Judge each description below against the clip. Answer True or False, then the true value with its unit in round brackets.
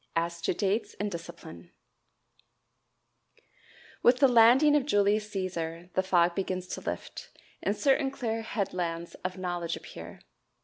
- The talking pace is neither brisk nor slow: False (130 wpm)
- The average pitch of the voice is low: False (190 Hz)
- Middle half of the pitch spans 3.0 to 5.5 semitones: True (4.6 semitones)